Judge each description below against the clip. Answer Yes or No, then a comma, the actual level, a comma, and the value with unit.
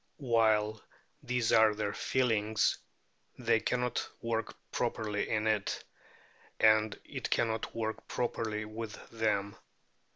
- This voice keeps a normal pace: No, slow, 105 wpm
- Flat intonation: Yes, narrow, 1.3 semitones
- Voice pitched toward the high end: No, low, 110 Hz